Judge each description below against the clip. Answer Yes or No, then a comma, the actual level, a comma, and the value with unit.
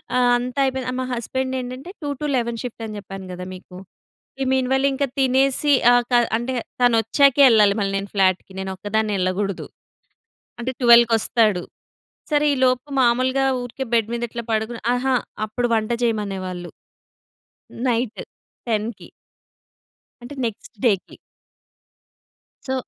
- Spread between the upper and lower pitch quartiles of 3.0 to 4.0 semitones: Yes, average, 3.7 semitones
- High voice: Yes, high, 235 Hz